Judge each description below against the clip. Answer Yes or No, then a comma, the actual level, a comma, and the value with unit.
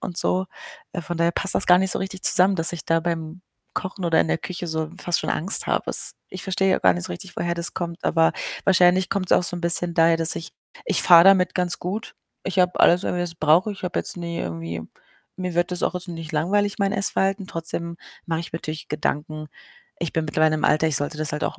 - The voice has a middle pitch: Yes, medium, 170 Hz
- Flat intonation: Yes, narrow, 2.2 semitones